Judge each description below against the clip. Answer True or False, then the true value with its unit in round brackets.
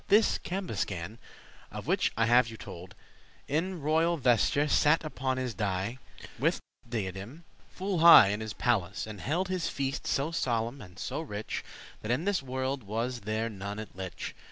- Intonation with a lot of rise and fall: True (6.4 semitones)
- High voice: False (120 Hz)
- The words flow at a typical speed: True (165 wpm)